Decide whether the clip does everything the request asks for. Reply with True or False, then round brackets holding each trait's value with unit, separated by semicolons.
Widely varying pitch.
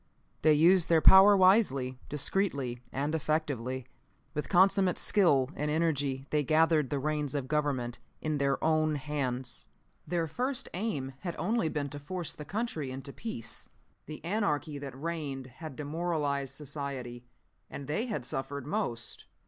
False (3.7 semitones)